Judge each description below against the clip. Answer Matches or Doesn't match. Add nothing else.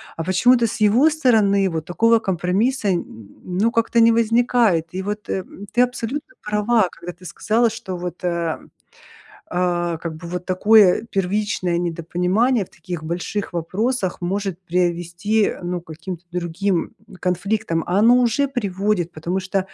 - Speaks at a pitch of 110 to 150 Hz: Doesn't match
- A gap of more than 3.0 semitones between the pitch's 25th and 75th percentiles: Matches